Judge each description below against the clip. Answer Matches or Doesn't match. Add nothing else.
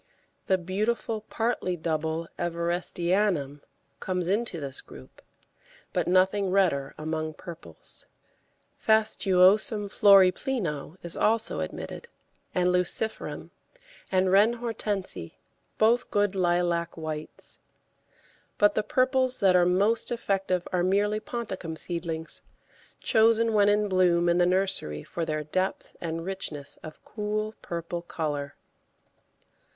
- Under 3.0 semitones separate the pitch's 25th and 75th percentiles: Doesn't match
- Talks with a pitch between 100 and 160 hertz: Doesn't match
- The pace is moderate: Doesn't match